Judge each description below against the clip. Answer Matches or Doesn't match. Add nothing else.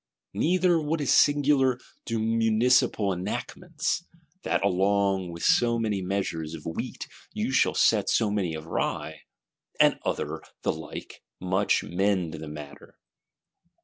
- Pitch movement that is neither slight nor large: Doesn't match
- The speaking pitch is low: Matches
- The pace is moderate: Doesn't match